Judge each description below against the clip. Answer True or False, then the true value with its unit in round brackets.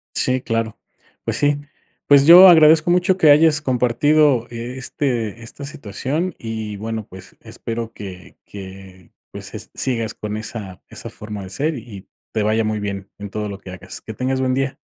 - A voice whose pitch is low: True (115 Hz)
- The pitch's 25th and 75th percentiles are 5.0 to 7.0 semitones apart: True (5.4 semitones)